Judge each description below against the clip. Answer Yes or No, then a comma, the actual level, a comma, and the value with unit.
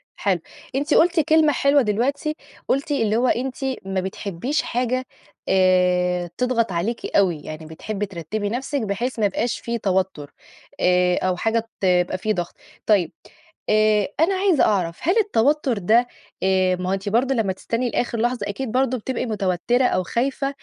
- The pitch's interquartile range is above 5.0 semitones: Yes, wide, 5.5 semitones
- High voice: Yes, high, 215 Hz